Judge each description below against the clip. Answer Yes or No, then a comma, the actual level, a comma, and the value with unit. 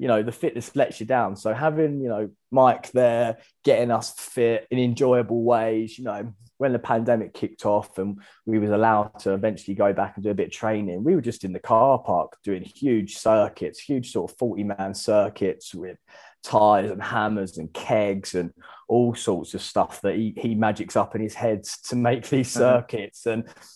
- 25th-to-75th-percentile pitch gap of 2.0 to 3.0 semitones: Yes, narrow, 2.5 semitones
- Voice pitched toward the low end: Yes, low, 110 Hz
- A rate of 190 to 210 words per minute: Yes, average, 200 wpm